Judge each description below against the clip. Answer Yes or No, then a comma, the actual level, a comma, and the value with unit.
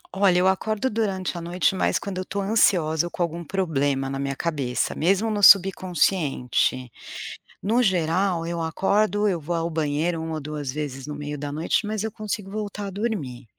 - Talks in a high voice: No, medium, 175 Hz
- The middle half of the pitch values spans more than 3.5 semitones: Yes, average, 4.9 semitones